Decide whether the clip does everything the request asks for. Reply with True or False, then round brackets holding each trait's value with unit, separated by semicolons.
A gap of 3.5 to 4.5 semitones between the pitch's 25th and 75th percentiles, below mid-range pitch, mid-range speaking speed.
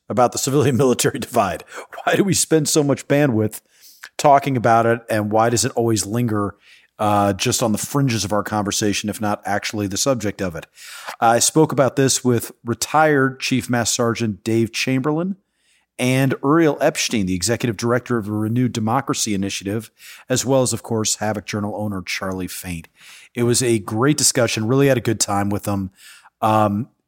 True (3.9 semitones; 115 Hz; 180 wpm)